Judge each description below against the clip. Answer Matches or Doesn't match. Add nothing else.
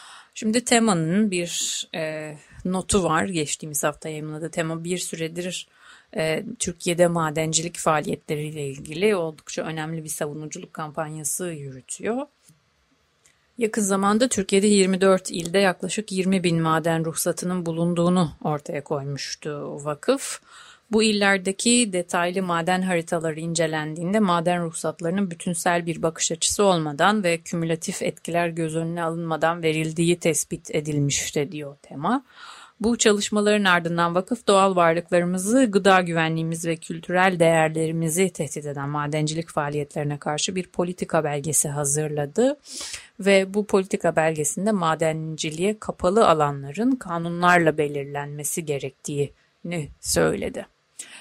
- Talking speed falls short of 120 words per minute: Matches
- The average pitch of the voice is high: Doesn't match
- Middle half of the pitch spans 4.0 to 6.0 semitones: Doesn't match